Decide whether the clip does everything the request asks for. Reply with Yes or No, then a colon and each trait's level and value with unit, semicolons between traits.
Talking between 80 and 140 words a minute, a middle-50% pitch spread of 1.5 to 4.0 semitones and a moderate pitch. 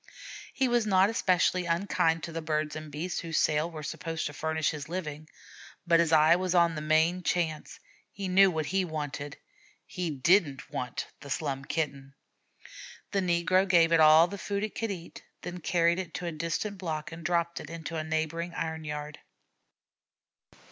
No: average, 180 wpm; narrow, 2.6 semitones; medium, 165 Hz